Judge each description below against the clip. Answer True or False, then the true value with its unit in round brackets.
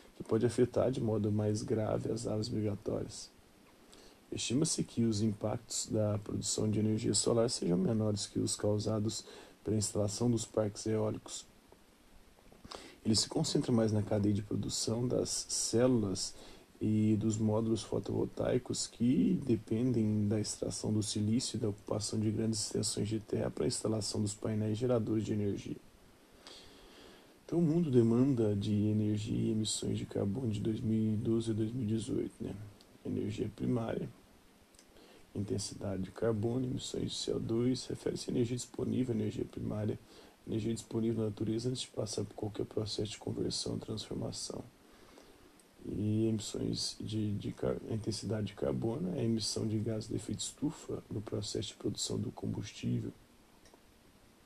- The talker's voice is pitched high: False (110 Hz)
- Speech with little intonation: True (1.4 semitones)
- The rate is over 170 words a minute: False (140 wpm)